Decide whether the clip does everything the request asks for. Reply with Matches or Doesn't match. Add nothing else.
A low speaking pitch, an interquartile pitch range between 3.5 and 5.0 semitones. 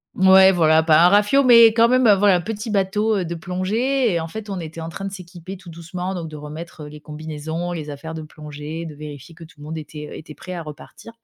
Doesn't match